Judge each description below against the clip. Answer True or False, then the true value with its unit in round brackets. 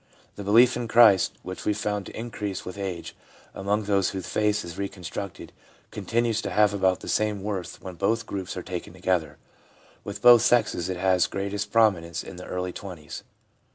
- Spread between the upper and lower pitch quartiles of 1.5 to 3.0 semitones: True (2.4 semitones)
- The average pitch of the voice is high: False (100 Hz)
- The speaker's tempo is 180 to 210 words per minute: True (185 wpm)